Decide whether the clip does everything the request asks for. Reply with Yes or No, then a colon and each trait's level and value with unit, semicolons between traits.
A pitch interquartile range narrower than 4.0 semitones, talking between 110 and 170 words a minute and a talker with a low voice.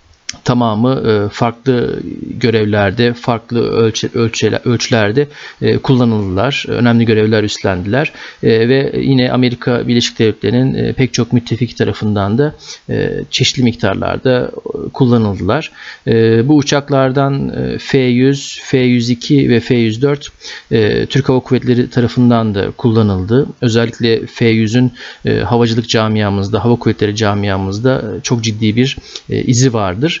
No: average, 2.8 semitones; slow, 95 wpm; low, 120 Hz